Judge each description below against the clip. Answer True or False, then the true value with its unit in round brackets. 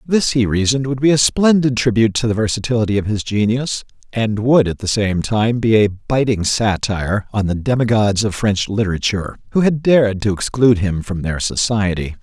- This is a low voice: True (110 Hz)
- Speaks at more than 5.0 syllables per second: True (5.4 syllables/s)